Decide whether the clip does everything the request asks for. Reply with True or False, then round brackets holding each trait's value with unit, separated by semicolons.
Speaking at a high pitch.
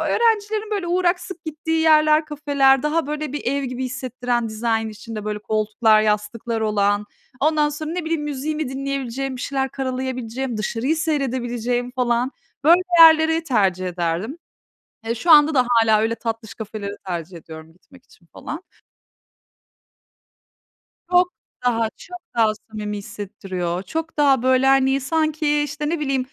True (260 Hz)